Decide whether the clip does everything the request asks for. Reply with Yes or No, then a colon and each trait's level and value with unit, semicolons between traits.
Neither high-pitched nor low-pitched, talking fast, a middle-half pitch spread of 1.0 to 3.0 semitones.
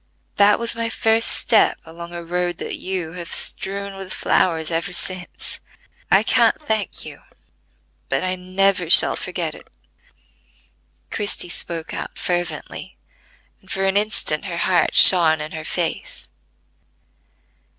No: medium, 180 Hz; slow, 135 wpm; narrow, 2.5 semitones